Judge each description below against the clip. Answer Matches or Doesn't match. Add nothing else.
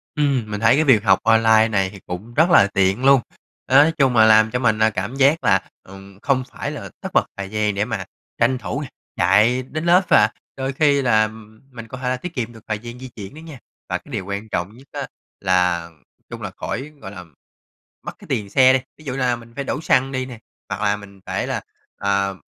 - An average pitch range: Matches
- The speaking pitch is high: Doesn't match